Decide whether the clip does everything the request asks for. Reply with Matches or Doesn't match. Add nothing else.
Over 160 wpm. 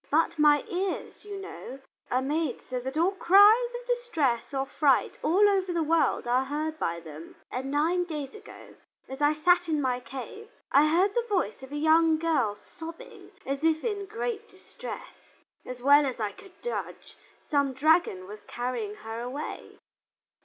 Matches